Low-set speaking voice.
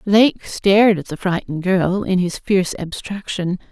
No: medium, 185 Hz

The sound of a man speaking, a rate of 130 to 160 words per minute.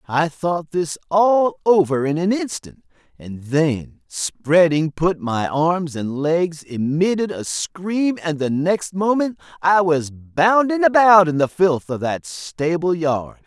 Yes: male; average, 150 wpm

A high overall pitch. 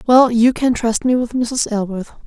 Yes: high, 235 Hz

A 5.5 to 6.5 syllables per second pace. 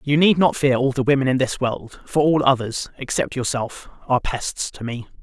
No: 5.1 syllables/s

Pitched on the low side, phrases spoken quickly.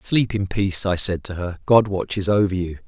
Yes: very low, 95 Hz; fast, 230 wpm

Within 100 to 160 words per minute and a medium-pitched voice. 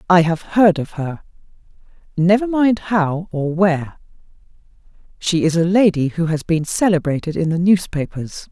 Yes: average, 140 wpm; medium, 175 Hz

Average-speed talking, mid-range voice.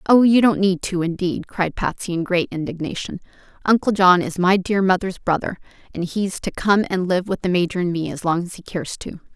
No: fast, 225 wpm; medium, 180 Hz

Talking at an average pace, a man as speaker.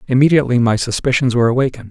Yes: average, 160 wpm; male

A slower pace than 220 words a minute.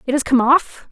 No: fast, 260 wpm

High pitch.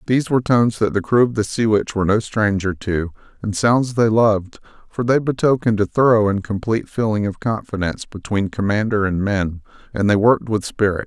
No: low, 105 Hz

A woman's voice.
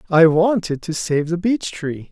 No: male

